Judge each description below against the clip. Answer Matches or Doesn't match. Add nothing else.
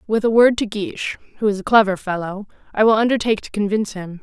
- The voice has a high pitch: Matches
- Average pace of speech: Doesn't match